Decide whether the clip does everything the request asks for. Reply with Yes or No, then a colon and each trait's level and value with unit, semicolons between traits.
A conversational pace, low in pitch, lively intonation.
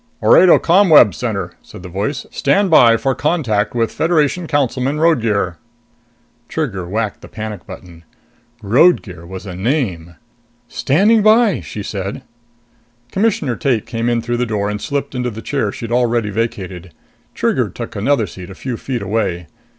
Yes: average, 150 wpm; low, 115 Hz; wide, 6.2 semitones